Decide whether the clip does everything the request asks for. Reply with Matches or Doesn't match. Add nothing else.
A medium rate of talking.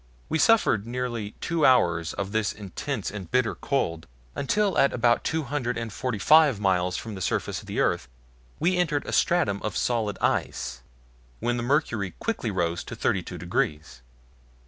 Matches